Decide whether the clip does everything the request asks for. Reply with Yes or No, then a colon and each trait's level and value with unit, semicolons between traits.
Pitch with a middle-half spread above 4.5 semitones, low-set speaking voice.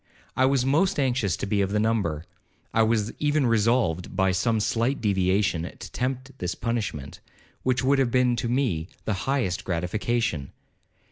Yes: wide, 5.4 semitones; low, 110 Hz